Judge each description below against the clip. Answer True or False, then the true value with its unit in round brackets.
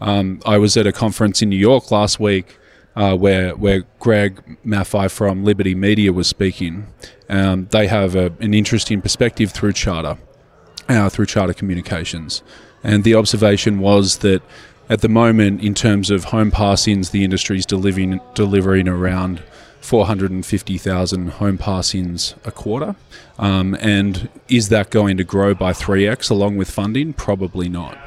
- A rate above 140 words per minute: True (155 wpm)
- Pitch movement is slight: True (2.0 semitones)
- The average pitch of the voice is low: True (100 Hz)